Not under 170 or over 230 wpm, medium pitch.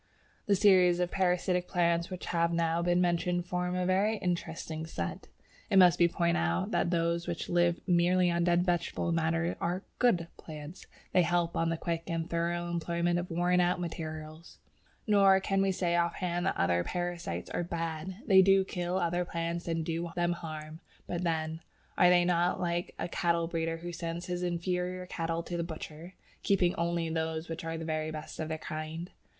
Yes: average, 190 wpm; medium, 170 Hz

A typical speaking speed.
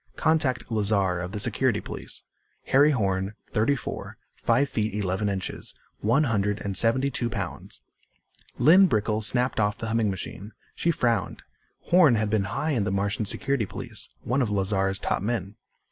Yes: average, 160 wpm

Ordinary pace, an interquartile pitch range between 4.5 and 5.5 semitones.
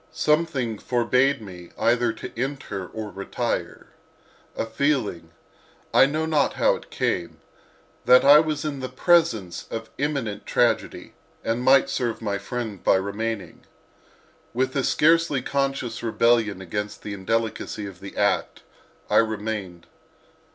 No: slow, 130 wpm; average, 5.0 semitones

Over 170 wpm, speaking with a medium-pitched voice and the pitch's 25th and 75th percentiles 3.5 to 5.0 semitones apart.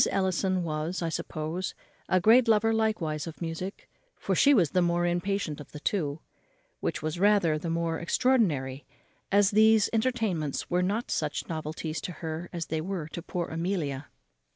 No: average, 165 wpm; medium, 175 Hz; average, 4.1 semitones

